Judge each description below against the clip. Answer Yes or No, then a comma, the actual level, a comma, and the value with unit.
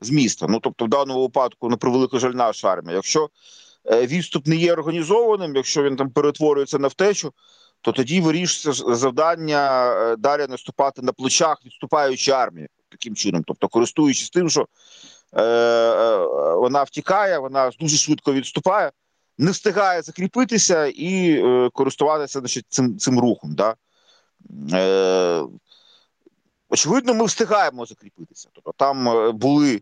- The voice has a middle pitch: Yes, medium, 145 Hz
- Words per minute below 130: No, average, 135 wpm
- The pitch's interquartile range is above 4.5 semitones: Yes, average, 5.1 semitones